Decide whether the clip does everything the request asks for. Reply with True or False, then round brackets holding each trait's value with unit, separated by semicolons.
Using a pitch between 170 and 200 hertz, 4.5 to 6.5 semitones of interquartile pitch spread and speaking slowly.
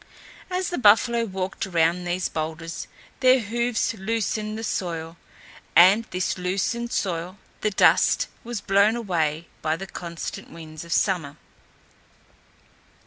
True (190 Hz; 4.9 semitones; 125 wpm)